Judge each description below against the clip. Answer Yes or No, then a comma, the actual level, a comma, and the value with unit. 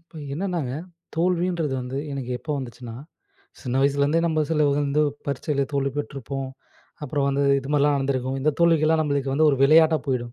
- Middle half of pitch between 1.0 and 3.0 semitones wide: Yes, narrow, 2.6 semitones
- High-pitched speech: No, medium, 140 Hz